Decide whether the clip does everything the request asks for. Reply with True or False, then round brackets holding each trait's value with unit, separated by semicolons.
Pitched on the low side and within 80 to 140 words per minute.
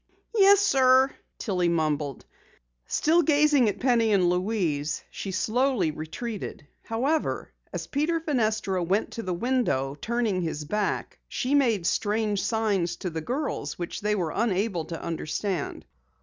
False (210 Hz; 135 wpm)